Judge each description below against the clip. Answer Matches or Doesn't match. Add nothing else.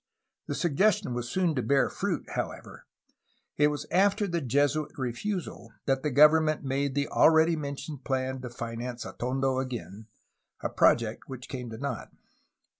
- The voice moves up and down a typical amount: Matches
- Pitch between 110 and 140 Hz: Matches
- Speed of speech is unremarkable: Matches